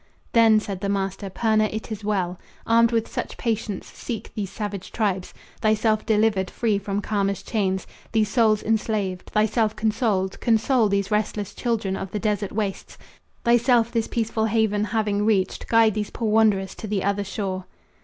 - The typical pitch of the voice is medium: No, high, 215 Hz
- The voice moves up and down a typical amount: No, narrow, 2.0 semitones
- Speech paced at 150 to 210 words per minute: Yes, average, 165 wpm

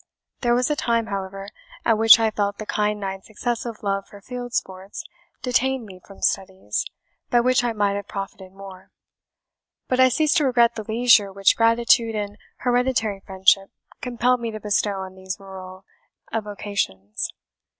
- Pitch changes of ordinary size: Yes, average, 3.5 semitones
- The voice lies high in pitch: Yes, high, 210 Hz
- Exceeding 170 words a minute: No, average, 160 wpm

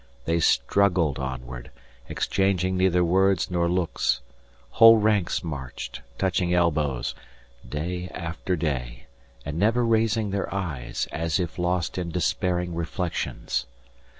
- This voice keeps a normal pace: No, slow, 115 wpm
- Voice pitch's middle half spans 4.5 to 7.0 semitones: No, average, 3.7 semitones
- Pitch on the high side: No, very low, 85 Hz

